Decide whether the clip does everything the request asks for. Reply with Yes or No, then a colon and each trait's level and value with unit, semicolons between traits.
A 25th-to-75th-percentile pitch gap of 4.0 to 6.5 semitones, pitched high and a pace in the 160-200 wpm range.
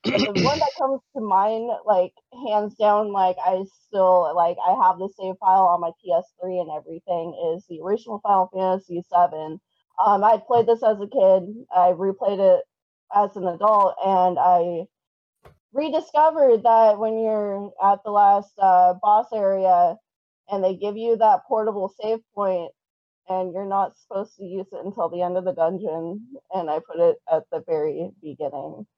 No: average, 3.5 semitones; high, 195 Hz; average, 175 wpm